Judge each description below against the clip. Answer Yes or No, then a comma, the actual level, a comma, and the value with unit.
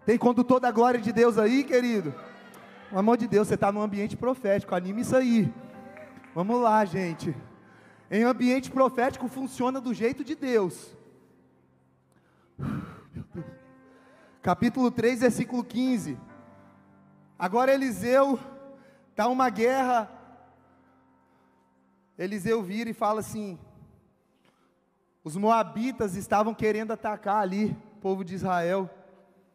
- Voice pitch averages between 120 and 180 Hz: No, high, 215 Hz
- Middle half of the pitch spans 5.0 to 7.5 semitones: Yes, average, 5.3 semitones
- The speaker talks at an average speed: No, slow, 115 wpm